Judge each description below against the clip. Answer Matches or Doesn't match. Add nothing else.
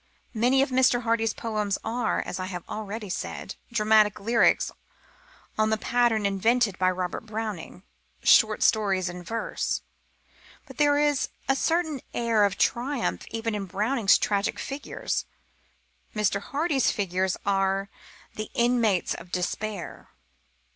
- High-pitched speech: Matches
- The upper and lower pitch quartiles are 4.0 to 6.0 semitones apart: Doesn't match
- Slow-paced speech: Matches